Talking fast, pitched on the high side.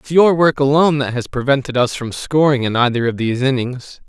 No: fast, 220 wpm; low, 135 Hz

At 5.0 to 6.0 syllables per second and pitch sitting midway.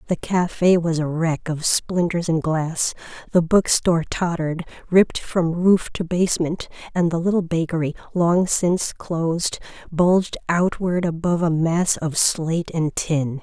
No: 4.5 syllables/s; medium, 170 Hz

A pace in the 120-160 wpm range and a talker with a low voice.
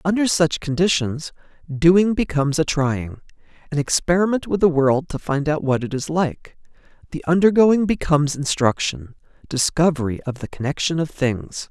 No: average, 145 wpm; medium, 155 Hz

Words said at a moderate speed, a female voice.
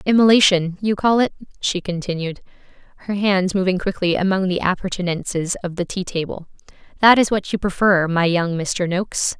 Yes: average, 165 wpm; female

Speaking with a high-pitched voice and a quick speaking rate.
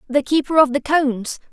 No: very high, 280 Hz; average, 195 wpm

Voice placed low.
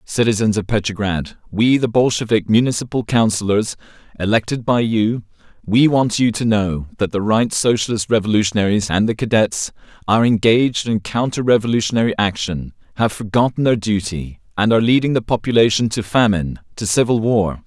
Yes: low, 110 Hz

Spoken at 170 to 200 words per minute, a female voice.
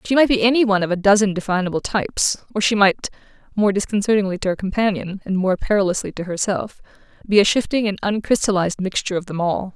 Yes: average, 185 wpm; female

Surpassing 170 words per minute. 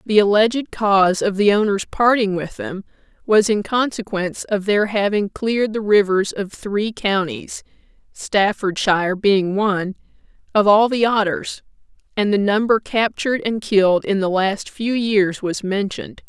No: average, 150 wpm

